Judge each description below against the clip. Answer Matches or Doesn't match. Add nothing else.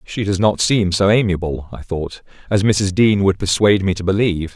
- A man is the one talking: Matches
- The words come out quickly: Matches